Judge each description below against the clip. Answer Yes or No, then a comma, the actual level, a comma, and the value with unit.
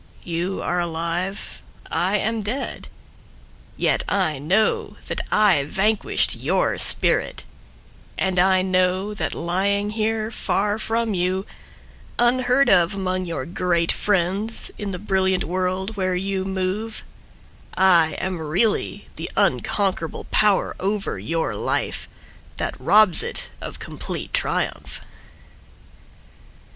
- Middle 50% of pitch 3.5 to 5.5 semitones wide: No, average, 2.7 semitones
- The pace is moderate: No, slow, 115 wpm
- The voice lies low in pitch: No, high, 190 Hz